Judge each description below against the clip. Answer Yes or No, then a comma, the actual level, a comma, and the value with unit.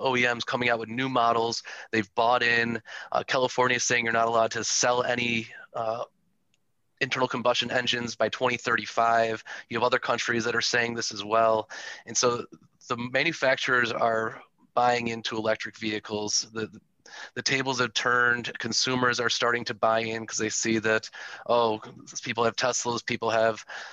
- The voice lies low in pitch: Yes, low, 115 Hz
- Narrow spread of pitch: Yes, narrow, 1.5 semitones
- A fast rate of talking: No, average, 165 wpm